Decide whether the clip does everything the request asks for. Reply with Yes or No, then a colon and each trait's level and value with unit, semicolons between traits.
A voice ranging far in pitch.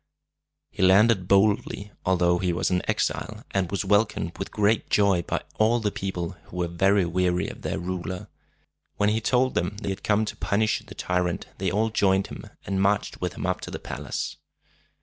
No: narrow, 2.4 semitones